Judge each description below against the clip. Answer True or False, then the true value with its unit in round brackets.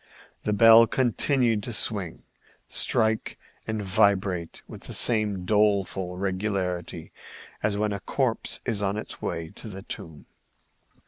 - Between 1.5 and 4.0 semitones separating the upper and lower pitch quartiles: True (2.8 semitones)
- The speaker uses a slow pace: True (130 wpm)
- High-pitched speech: False (105 Hz)